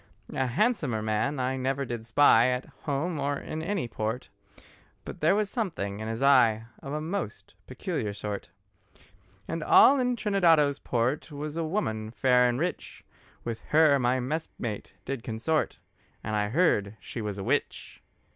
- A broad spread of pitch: Yes, wide, 5.9 semitones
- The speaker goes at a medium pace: Yes, average, 160 wpm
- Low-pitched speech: Yes, low, 130 Hz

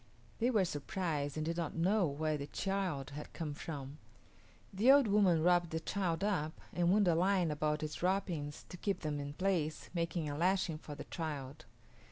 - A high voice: No, medium, 165 Hz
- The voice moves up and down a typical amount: Yes, average, 4.1 semitones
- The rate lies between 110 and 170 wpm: No, average, 190 wpm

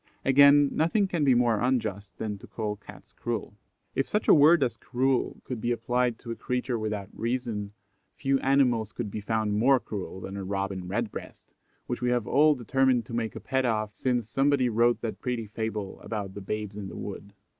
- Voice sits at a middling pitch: No, low, 115 Hz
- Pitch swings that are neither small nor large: Yes, average, 3.6 semitones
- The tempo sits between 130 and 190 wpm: No, average, 200 wpm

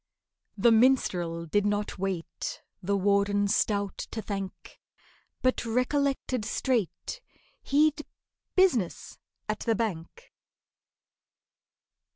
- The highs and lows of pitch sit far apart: No, average, 4.5 semitones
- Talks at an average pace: No, slow, 90 wpm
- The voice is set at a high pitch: Yes, high, 210 Hz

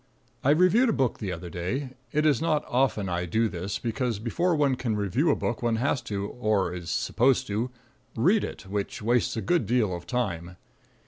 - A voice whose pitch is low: Yes, low, 115 Hz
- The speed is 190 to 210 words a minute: Yes, average, 200 wpm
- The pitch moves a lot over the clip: Yes, wide, 5.7 semitones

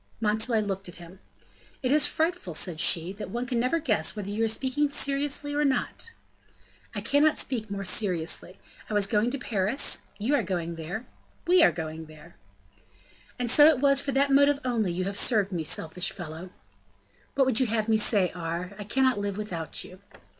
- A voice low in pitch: No, high, 215 Hz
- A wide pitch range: Yes, wide, 6.5 semitones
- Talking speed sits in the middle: Yes, average, 190 wpm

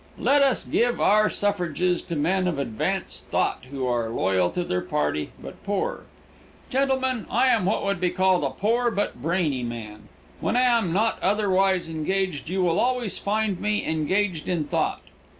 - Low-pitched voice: No, medium, 185 Hz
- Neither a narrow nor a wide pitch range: No, wide, 5.7 semitones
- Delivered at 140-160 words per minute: No, average, 170 wpm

